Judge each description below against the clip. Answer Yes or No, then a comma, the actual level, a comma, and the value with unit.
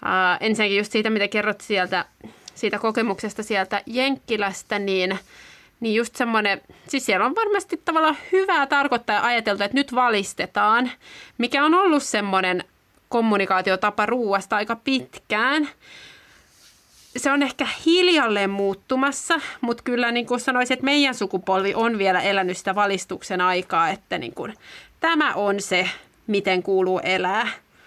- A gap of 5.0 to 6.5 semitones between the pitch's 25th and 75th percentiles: Yes, average, 5.3 semitones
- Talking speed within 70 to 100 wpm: No, average, 135 wpm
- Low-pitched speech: No, high, 220 Hz